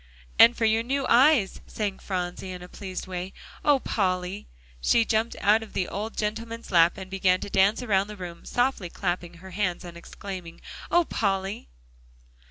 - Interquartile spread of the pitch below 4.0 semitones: Yes, average, 3.6 semitones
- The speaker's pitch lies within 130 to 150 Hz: No, high, 195 Hz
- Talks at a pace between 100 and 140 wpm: No, average, 175 wpm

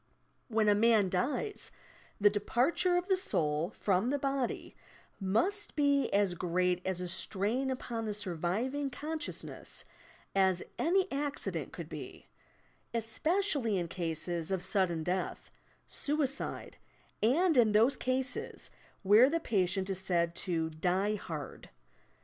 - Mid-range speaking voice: No, high, 210 Hz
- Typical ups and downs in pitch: No, wide, 7.1 semitones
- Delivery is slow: Yes, slow, 125 wpm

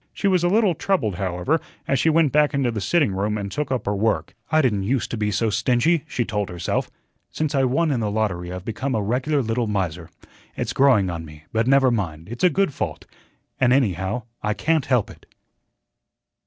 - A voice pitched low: Yes, low, 115 Hz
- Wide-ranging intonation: Yes, wide, 5.9 semitones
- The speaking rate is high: Yes, fast, 210 wpm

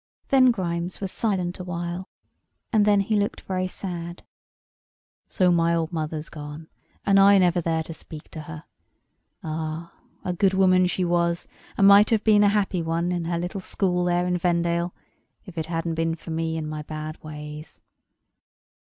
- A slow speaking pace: No, average, 170 wpm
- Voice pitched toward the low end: No, medium, 175 Hz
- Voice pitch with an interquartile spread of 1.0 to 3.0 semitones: Yes, narrow, 2.4 semitones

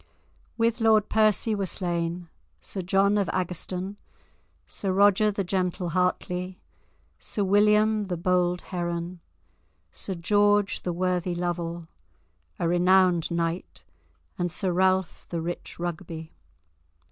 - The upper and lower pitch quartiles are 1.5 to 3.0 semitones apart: Yes, narrow, 2.4 semitones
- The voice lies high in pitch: No, medium, 180 Hz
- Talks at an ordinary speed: No, slow, 115 wpm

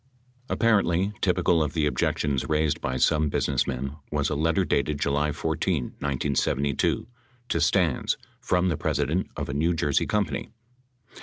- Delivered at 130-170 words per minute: Yes, average, 140 wpm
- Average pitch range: Yes, average, 3.4 semitones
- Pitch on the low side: Yes, very low, 75 Hz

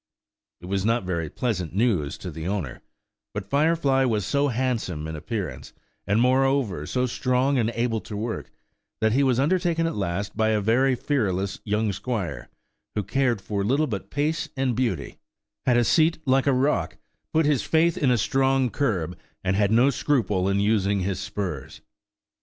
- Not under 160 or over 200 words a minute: Yes, average, 175 wpm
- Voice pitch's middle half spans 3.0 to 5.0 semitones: No, wide, 5.4 semitones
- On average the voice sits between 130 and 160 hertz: No, low, 115 Hz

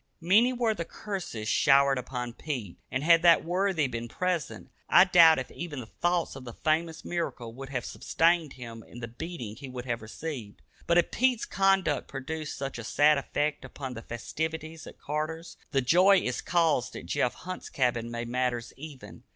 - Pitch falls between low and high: Yes, medium, 150 Hz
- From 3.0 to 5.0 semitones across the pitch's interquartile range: No, wide, 5.5 semitones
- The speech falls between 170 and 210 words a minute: Yes, average, 185 wpm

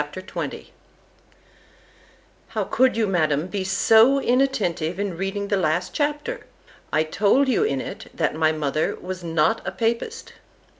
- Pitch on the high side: Yes, high, 195 Hz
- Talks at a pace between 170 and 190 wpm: No, average, 140 wpm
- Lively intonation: Yes, wide, 6.8 semitones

